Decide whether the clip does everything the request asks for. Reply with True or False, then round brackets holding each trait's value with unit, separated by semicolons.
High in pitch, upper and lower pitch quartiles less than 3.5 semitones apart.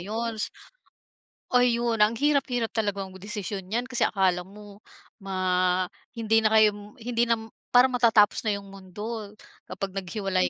True (210 Hz; 3.0 semitones)